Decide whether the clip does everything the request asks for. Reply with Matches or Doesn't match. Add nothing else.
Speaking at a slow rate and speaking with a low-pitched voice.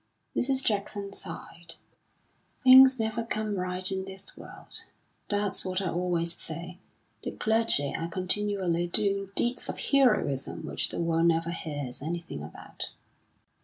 Doesn't match